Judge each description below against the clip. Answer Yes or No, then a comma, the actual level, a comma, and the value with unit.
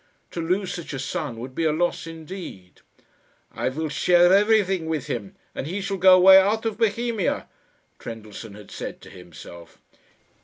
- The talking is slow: No, average, 165 wpm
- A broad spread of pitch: Yes, wide, 7.0 semitones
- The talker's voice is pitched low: No, medium, 170 Hz